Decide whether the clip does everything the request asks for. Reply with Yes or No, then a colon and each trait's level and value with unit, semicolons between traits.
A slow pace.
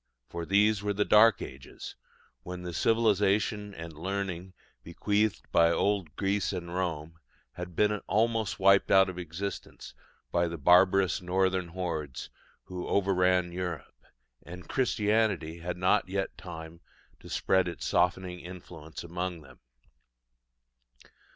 Yes: slow, 125 wpm